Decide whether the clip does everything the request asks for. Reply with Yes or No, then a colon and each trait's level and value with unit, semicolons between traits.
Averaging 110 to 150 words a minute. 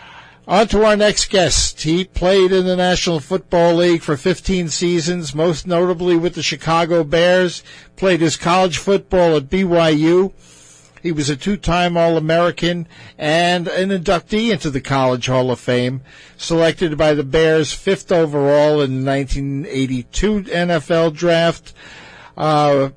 Yes: average, 140 wpm